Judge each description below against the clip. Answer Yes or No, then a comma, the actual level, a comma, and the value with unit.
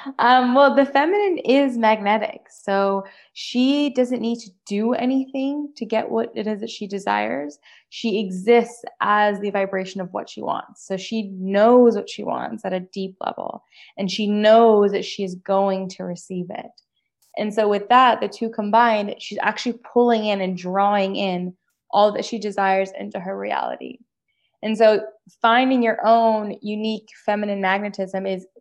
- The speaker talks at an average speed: Yes, average, 170 wpm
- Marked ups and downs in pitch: No, average, 3.1 semitones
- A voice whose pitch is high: Yes, high, 210 Hz